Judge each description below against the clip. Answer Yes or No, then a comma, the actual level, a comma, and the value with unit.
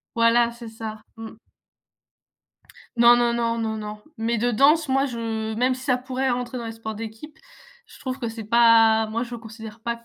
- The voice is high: Yes, high, 230 Hz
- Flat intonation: Yes, narrow, 1.6 semitones